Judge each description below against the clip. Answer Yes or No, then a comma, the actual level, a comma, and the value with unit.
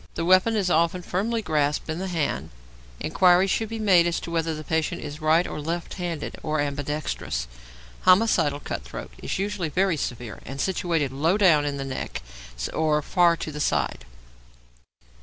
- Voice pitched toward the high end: No, medium, 165 Hz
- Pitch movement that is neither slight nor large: Yes, average, 3.7 semitones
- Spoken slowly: No, average, 175 wpm